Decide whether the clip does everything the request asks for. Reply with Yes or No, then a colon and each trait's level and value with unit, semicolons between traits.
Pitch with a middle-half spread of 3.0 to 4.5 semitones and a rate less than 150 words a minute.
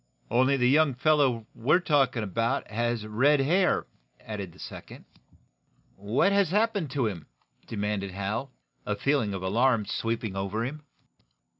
No: wide, 5.4 semitones; average, 140 wpm